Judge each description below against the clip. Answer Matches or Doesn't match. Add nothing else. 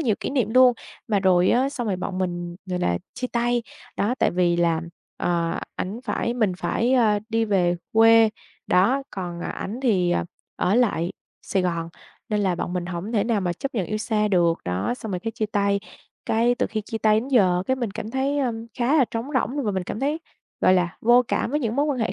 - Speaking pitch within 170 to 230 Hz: Matches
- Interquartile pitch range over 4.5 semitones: Matches